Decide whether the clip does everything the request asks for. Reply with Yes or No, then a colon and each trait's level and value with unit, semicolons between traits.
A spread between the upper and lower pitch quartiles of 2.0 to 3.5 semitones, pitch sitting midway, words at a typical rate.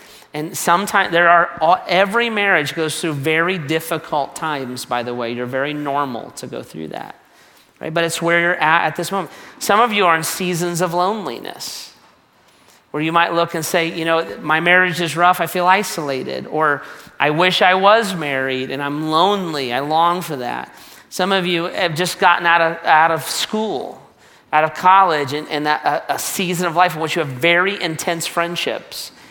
Yes: average, 2.8 semitones; medium, 170 Hz; average, 195 wpm